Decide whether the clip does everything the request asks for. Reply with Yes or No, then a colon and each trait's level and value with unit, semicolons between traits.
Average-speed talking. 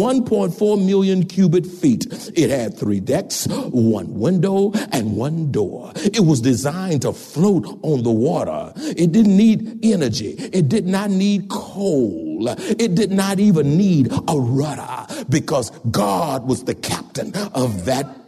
Yes: average, 145 wpm